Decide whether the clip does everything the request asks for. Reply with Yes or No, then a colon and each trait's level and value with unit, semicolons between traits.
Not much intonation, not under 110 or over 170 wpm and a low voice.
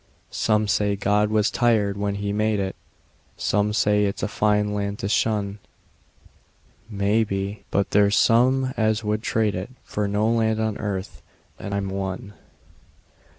Yes: narrow, 1.4 semitones; average, 150 wpm; low, 105 Hz